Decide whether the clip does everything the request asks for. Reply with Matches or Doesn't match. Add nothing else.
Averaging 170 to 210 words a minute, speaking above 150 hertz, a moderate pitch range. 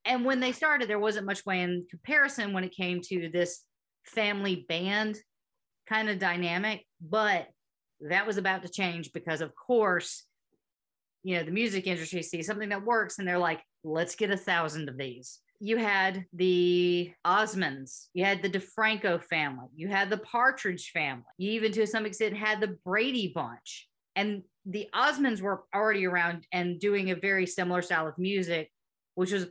Matches